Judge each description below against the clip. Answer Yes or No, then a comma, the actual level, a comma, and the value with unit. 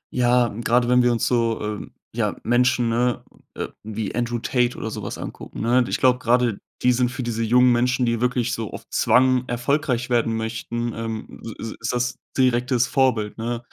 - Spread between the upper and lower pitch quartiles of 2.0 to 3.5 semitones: No, narrow, 1.5 semitones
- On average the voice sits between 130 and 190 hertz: No, low, 120 Hz